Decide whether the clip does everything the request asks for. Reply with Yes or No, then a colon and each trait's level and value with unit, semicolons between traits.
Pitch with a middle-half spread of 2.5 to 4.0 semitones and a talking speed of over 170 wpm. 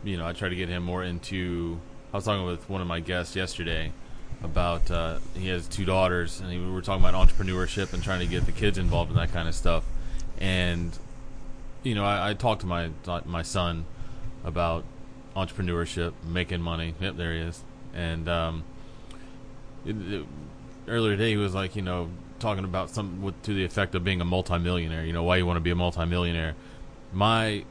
Yes: average, 3.1 semitones; average, 195 wpm